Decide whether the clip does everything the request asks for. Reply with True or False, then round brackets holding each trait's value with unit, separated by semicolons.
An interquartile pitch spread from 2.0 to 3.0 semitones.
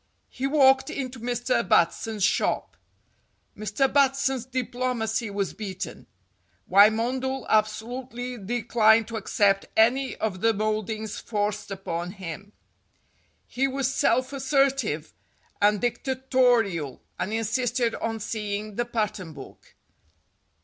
False (3.7 semitones)